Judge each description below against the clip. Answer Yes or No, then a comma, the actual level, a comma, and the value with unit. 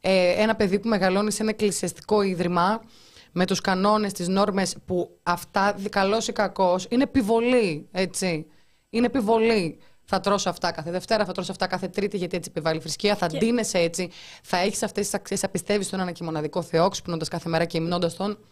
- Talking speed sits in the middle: No, fast, 230 wpm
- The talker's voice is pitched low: No, high, 190 Hz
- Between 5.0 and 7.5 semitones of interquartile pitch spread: No, average, 3.0 semitones